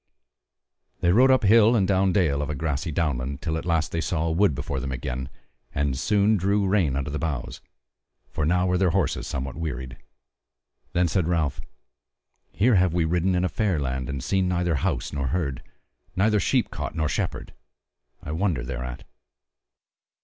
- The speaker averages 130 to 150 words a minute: No, average, 175 wpm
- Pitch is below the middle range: Yes, very low, 80 Hz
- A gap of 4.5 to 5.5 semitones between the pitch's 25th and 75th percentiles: Yes, average, 5.1 semitones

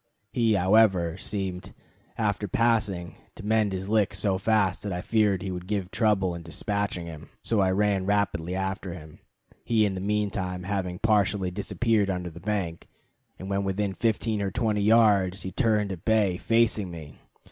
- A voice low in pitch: Yes, low, 100 Hz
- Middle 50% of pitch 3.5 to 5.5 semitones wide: No, narrow, 2.4 semitones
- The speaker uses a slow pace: No, average, 175 wpm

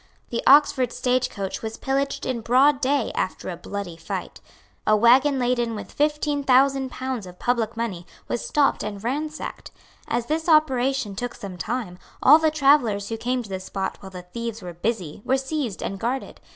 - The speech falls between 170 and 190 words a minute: Yes, average, 180 wpm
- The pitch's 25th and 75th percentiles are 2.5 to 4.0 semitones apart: No, average, 5.1 semitones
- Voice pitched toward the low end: No, high, 245 Hz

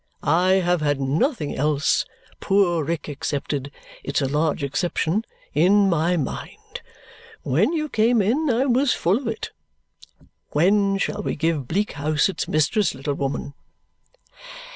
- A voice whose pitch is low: No, medium, 170 Hz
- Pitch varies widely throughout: Yes, wide, 5.9 semitones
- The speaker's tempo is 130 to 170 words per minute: Yes, average, 140 wpm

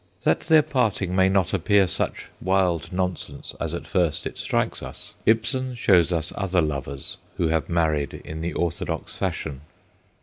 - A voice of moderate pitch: No, very low, 90 Hz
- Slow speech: No, average, 160 wpm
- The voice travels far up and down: No, average, 3.4 semitones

